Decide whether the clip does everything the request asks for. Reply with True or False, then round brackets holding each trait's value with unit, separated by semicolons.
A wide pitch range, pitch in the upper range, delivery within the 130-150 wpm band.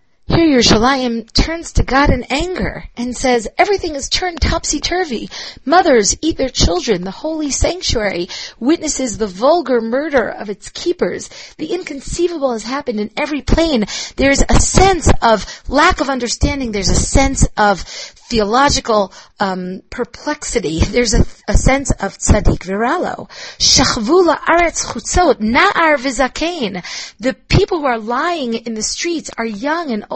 True (5.8 semitones; 265 Hz; 145 wpm)